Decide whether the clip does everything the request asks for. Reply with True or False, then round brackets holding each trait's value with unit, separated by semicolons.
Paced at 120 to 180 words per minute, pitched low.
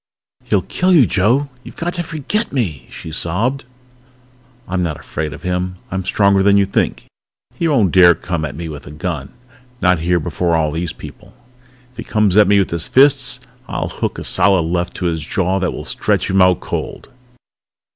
False (195 wpm; 90 Hz)